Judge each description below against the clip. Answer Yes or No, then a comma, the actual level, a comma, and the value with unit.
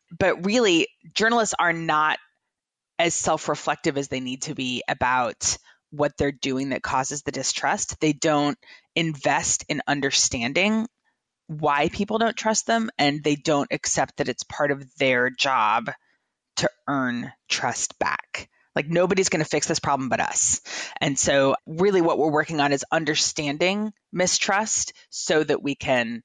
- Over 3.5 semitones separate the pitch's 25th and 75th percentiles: Yes, average, 4.3 semitones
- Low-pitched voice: No, medium, 155 Hz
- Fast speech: No, average, 155 wpm